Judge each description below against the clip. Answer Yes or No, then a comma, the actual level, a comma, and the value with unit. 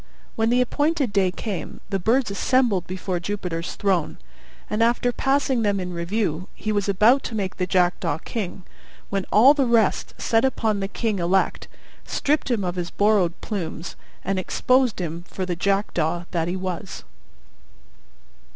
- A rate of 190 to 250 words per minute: No, average, 160 wpm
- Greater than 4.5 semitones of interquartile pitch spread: No, average, 4.1 semitones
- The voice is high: Yes, high, 200 Hz